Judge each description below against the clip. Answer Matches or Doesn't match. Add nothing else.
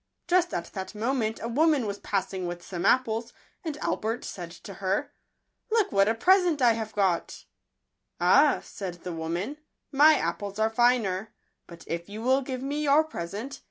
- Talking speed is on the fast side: Doesn't match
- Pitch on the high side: Matches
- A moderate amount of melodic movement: Doesn't match